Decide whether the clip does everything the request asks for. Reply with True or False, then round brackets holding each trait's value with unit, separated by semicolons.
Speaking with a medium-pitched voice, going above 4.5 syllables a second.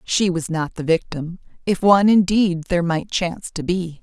True (175 Hz; 5.0 syllables/s)